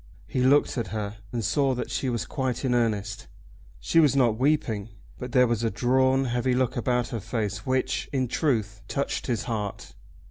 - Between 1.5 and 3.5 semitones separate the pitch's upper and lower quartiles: Yes, average, 2.8 semitones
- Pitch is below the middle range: Yes, low, 125 Hz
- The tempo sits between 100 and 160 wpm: No, average, 185 wpm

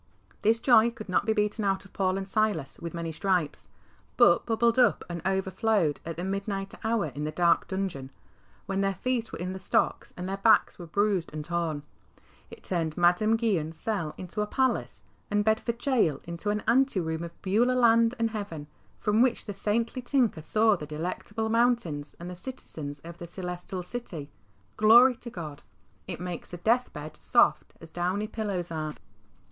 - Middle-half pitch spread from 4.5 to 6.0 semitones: Yes, average, 4.8 semitones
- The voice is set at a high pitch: Yes, high, 195 Hz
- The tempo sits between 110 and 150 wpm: No, average, 185 wpm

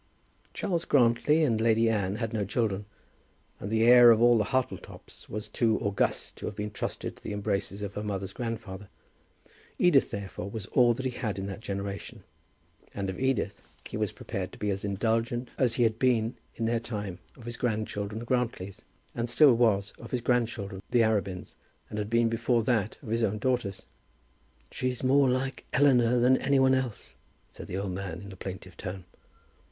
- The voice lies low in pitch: Yes, low, 115 Hz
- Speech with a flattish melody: No, average, 3.3 semitones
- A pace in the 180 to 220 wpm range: Yes, average, 190 wpm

